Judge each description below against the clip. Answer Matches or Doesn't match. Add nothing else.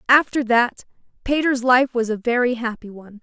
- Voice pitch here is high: Matches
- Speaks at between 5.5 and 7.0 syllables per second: Doesn't match